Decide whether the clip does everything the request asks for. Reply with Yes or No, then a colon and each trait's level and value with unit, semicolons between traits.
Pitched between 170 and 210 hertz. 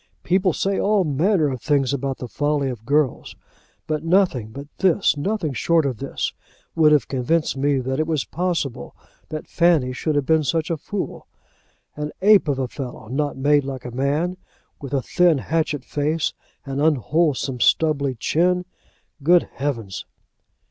No: medium, 145 Hz